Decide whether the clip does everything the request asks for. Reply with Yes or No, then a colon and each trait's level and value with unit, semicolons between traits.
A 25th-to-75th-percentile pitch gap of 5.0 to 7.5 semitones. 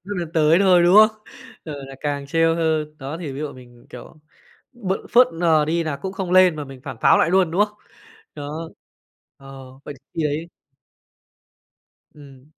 No: average, 3.7 semitones